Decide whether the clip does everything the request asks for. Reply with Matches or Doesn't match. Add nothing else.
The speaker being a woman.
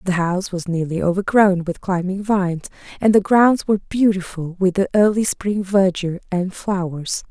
Matches